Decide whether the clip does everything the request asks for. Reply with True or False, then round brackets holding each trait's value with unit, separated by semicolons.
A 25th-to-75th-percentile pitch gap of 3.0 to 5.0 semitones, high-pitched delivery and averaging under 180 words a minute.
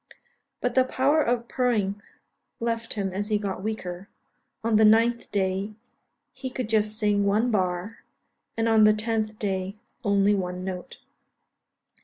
False (2.6 semitones; 215 Hz; 145 wpm)